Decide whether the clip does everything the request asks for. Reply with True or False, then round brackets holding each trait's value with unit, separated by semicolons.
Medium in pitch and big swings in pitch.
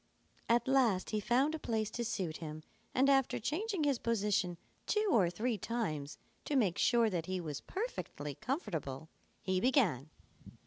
False (220 Hz; 7.2 semitones)